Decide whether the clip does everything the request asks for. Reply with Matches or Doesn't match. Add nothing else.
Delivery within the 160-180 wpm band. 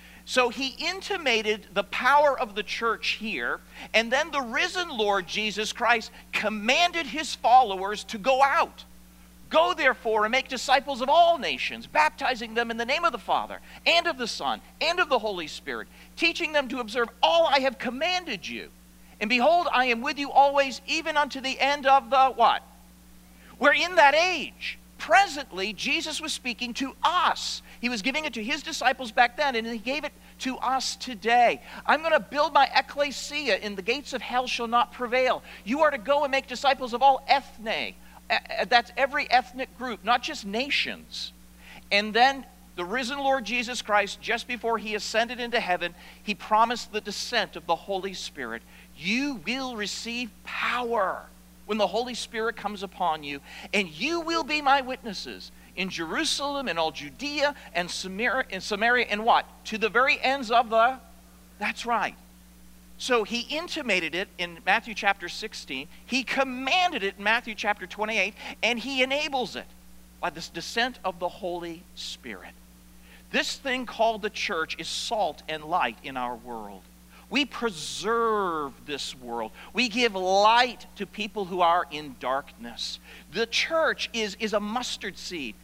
Matches